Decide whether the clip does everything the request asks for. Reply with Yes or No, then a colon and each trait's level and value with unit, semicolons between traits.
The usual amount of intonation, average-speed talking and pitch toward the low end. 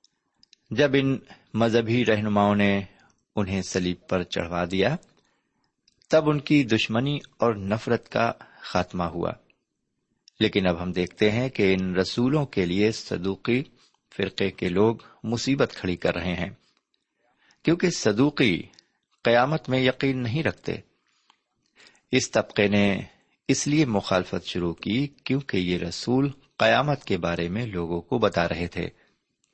No: wide, 5.9 semitones; average, 130 wpm; low, 110 Hz